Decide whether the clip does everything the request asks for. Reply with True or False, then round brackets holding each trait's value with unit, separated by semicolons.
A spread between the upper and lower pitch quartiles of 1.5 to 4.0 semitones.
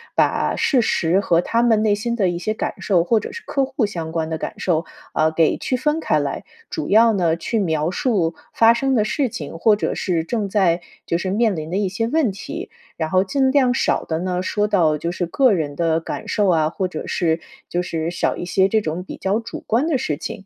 False (5.3 semitones)